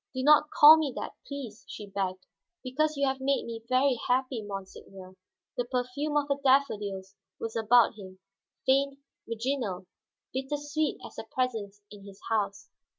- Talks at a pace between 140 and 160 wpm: Yes, average, 155 wpm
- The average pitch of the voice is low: No, very high, 250 Hz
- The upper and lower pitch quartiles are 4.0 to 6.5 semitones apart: Yes, wide, 5.4 semitones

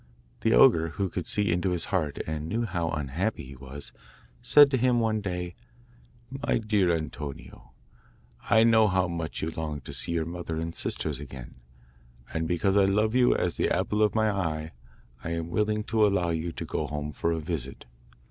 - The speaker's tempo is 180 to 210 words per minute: Yes, average, 190 wpm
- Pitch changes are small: No, average, 5.1 semitones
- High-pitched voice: No, very low, 85 Hz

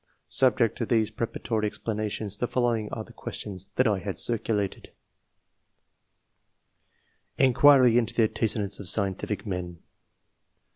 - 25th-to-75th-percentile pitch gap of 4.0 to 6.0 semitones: No, average, 2.7 semitones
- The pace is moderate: No, slow, 125 wpm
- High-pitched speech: No, low, 110 Hz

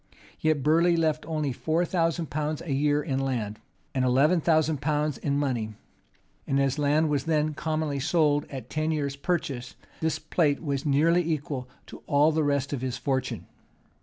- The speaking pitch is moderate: Yes, medium, 150 Hz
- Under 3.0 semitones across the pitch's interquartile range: Yes, narrow, 2.5 semitones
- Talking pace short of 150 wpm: No, average, 170 wpm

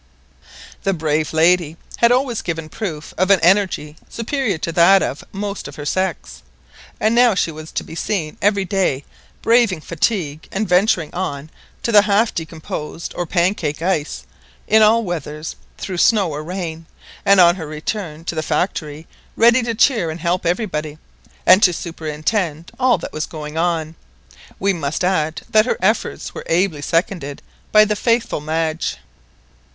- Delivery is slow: No, average, 160 wpm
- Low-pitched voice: No, medium, 175 Hz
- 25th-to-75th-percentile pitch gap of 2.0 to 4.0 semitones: No, average, 4.5 semitones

